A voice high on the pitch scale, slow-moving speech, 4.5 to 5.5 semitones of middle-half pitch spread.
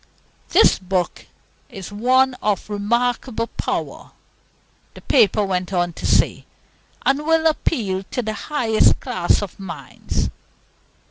Yes: high, 210 Hz; slow, 120 wpm; average, 5.0 semitones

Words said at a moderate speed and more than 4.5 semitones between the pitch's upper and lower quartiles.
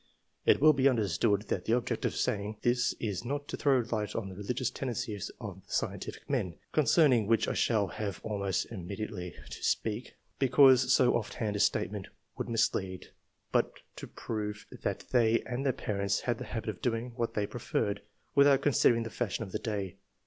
No: average, 190 wpm; average, 3.5 semitones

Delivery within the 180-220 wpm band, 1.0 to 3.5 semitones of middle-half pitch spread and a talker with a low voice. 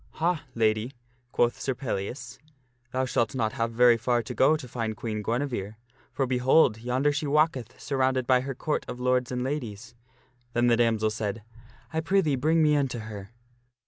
Yes: average, 190 wpm; average, 2.8 semitones; low, 125 Hz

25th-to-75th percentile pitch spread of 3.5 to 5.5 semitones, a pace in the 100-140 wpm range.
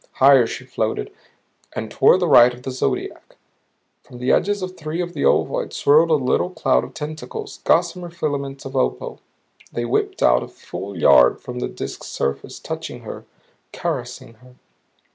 No: average, 5.2 semitones; average, 165 wpm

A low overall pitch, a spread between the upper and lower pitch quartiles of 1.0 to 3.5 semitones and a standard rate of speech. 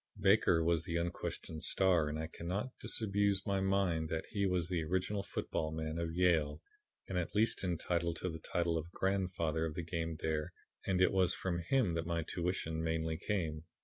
Yes: very low, 85 Hz; narrow, 2.6 semitones; average, 185 wpm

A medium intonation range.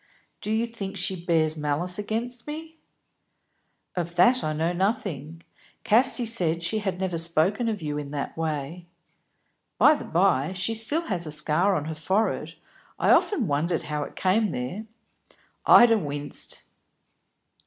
No: wide, 5.9 semitones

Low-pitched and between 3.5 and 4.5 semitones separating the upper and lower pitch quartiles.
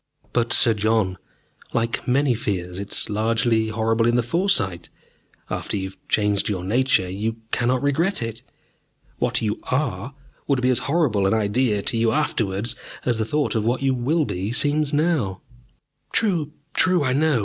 No: low, 115 Hz; average, 4.9 semitones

